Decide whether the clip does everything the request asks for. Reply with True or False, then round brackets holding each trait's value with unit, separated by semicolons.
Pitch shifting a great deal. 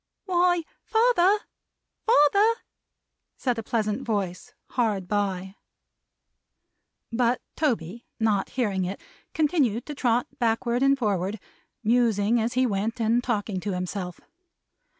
False (4.2 semitones)